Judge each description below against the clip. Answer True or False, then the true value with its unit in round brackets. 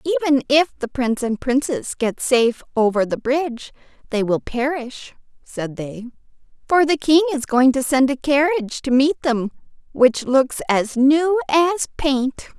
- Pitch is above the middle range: True (270 Hz)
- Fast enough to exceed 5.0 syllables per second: False (4.6 syllables/s)